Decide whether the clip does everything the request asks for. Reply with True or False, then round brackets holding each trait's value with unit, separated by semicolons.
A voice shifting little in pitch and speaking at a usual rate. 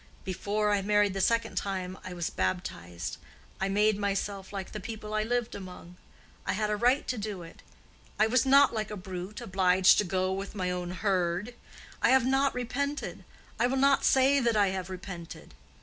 False (3.7 semitones; 190 wpm)